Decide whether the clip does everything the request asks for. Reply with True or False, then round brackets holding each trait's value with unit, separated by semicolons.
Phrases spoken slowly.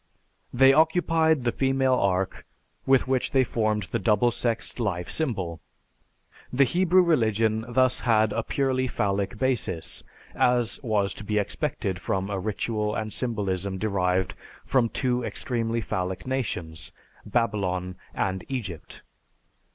True (130 wpm)